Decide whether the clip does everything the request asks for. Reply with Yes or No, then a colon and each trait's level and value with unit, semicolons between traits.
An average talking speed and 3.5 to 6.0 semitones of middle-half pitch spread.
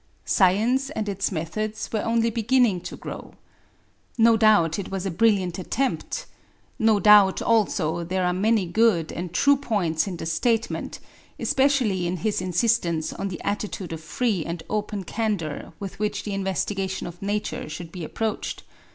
Yes: average, 160 wpm; average, 4.0 semitones